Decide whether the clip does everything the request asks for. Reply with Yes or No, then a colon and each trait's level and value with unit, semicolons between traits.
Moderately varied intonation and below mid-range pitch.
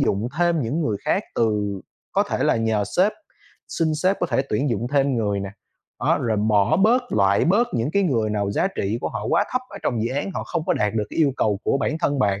No: wide, 7.6 semitones; low, 120 Hz